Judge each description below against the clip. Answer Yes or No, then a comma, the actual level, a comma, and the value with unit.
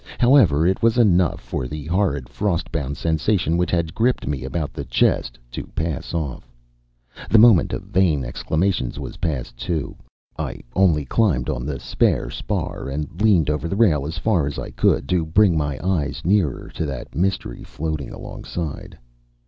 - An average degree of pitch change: Yes, average, 4.8 semitones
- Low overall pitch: Yes, very low, 80 Hz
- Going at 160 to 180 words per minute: Yes, average, 170 wpm